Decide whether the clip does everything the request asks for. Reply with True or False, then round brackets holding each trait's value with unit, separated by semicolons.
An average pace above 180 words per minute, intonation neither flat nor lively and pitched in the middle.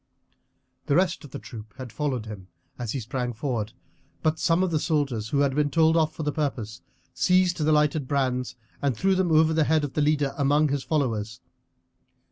True (200 wpm; 4.0 semitones; 145 Hz)